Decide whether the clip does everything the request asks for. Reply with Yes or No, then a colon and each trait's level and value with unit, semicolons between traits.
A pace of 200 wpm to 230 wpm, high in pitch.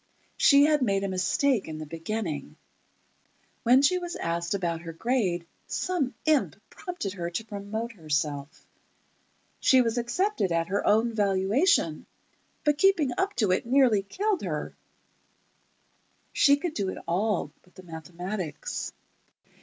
No: average, 140 wpm; high, 205 Hz